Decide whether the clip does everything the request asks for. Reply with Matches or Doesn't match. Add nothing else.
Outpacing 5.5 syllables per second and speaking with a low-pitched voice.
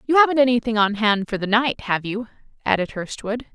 Doesn't match